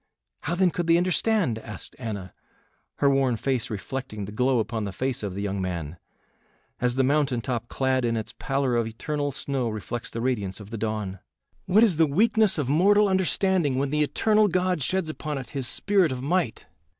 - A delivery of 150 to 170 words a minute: No, average, 195 wpm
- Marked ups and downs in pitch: Yes, wide, 6.9 semitones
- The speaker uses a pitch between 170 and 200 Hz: No, low, 135 Hz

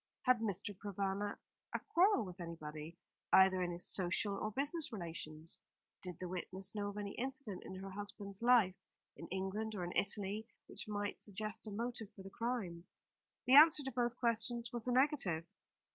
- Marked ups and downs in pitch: No, average, 4.1 semitones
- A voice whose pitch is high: Yes, high, 205 Hz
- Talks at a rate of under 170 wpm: No, average, 175 wpm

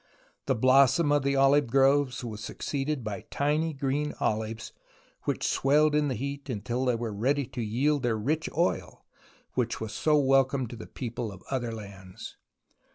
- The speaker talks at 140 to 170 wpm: Yes, average, 165 wpm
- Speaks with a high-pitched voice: No, low, 130 Hz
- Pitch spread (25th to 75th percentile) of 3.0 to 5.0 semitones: Yes, average, 4.0 semitones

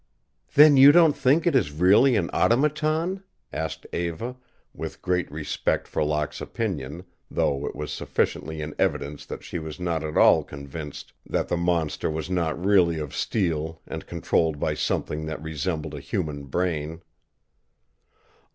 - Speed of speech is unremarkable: Yes, average, 150 wpm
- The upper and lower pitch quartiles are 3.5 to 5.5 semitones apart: Yes, average, 5.2 semitones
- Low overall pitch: Yes, very low, 85 Hz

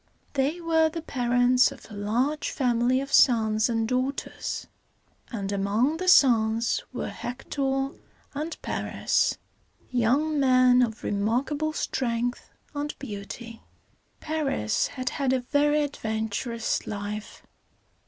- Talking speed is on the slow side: Yes, slow, 115 wpm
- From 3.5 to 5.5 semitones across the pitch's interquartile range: Yes, average, 4.1 semitones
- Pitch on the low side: No, very high, 250 Hz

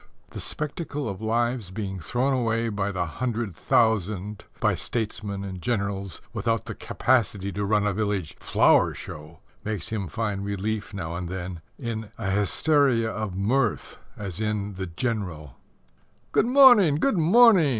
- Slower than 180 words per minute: Yes, average, 150 wpm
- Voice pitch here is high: No, low, 105 Hz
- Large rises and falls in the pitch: No, average, 3.7 semitones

